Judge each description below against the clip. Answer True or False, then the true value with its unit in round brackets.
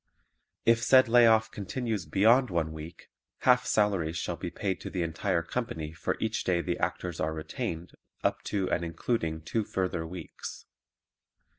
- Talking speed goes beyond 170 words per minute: False (160 wpm)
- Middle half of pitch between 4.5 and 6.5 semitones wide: True (5.4 semitones)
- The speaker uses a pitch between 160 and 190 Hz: False (90 Hz)